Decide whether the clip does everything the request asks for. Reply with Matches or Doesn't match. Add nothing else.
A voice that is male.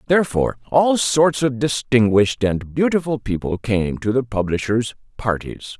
Matches